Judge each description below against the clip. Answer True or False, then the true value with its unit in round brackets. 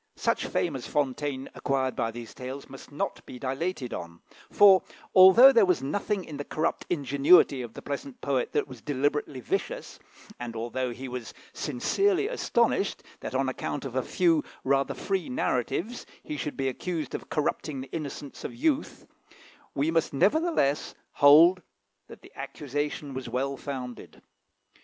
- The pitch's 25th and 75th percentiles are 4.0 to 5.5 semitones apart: True (5.0 semitones)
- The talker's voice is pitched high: False (140 Hz)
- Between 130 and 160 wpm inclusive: True (155 wpm)